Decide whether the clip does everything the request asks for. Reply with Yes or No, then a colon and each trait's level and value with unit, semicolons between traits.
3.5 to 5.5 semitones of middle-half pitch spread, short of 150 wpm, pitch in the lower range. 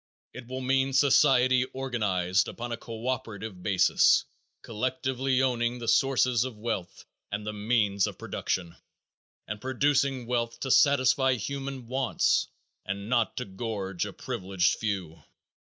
Yes: average, 4.0 semitones; slow, 135 wpm; low, 120 Hz